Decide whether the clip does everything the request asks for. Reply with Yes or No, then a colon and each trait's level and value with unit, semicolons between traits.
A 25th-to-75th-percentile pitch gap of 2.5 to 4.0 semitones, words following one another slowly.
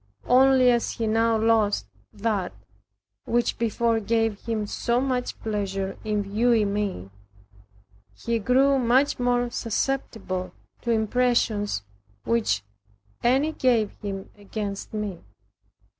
Yes: average, 3.0 semitones; slow, 110 wpm